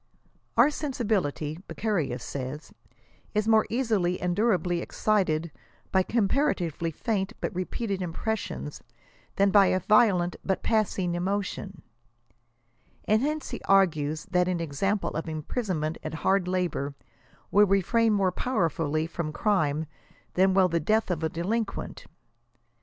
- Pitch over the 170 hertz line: Yes, medium, 185 Hz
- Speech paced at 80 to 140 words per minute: Yes, slow, 135 wpm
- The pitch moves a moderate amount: Yes, average, 4.7 semitones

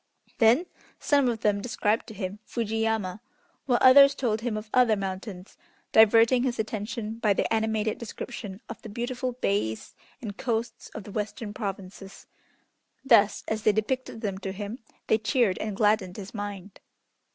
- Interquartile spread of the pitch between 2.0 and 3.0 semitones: Yes, narrow, 2.5 semitones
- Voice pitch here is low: No, high, 215 Hz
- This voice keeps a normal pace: Yes, average, 160 wpm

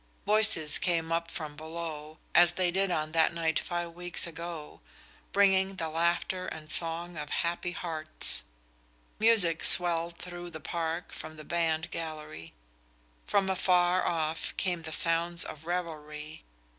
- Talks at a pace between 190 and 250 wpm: No, average, 140 wpm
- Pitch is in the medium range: Yes, medium, 170 Hz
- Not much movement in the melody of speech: Yes, narrow, 1.9 semitones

